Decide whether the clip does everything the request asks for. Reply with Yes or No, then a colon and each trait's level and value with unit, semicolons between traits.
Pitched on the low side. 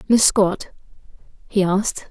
No: high, 200 Hz